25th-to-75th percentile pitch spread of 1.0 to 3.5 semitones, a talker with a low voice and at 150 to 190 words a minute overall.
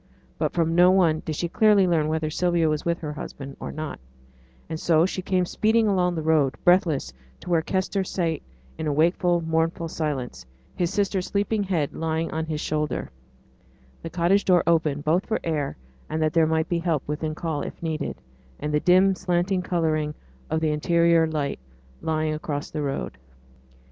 No: narrow, 2.5 semitones; medium, 165 Hz; average, 180 wpm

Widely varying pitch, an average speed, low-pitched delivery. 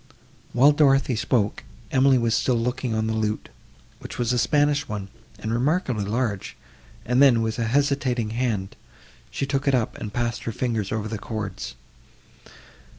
No: average, 3.4 semitones; average, 160 wpm; low, 120 Hz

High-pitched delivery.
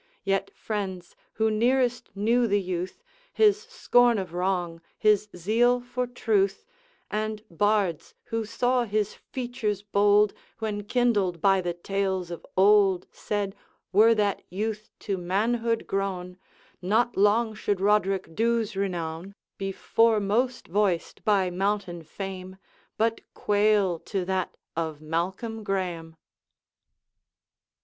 Yes: high, 205 Hz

